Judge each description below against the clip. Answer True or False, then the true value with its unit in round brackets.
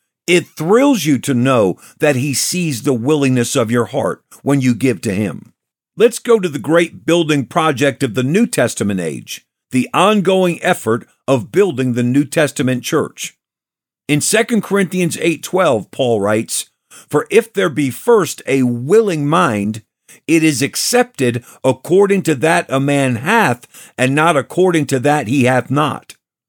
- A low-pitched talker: False (145 Hz)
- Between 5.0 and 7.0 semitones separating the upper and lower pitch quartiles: True (5.3 semitones)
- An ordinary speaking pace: True (160 wpm)